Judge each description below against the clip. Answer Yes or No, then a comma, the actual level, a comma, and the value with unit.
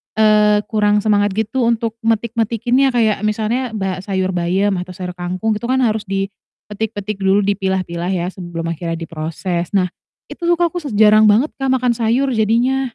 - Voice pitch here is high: Yes, high, 210 Hz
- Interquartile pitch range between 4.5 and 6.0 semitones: No, average, 3.3 semitones